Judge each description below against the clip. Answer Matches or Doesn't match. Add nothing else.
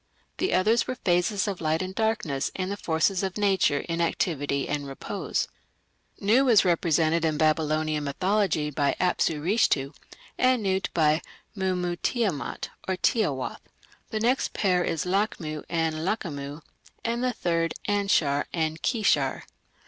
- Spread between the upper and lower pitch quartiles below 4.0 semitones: Doesn't match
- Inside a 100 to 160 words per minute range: Matches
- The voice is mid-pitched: Matches